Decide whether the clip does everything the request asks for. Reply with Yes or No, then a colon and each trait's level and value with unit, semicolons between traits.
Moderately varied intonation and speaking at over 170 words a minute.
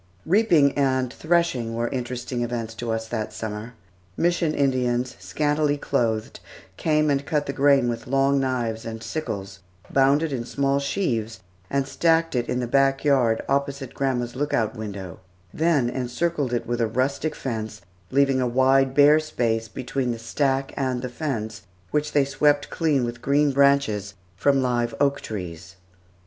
No: average, 3.3 semitones; average, 160 wpm